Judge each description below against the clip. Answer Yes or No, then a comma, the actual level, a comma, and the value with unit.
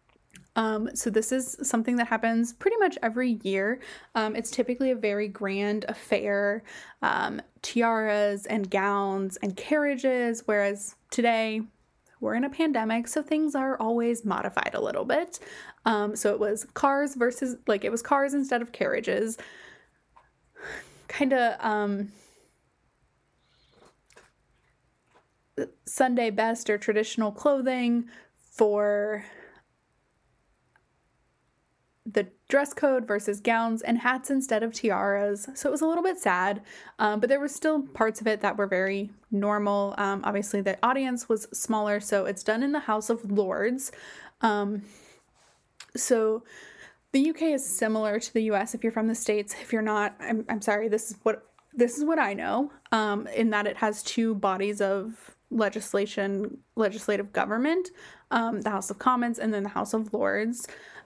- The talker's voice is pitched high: Yes, high, 225 Hz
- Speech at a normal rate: Yes, average, 150 wpm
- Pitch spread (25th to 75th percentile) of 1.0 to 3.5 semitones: Yes, average, 3.2 semitones